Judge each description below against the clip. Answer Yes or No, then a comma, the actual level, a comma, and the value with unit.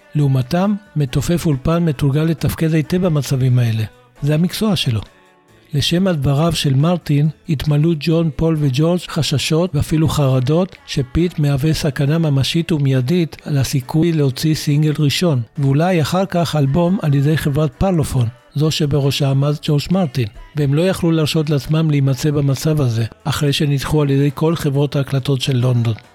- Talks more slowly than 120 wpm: No, average, 140 wpm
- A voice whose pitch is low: No, medium, 150 Hz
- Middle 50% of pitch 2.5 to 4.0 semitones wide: Yes, average, 2.8 semitones